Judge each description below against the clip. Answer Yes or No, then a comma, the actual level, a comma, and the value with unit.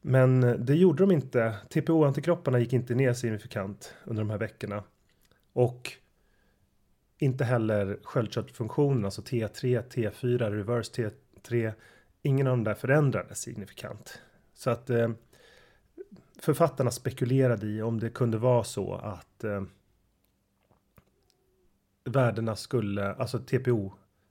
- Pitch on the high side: No, low, 120 Hz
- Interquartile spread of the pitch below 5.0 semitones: Yes, average, 3.5 semitones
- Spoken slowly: Yes, slow, 110 wpm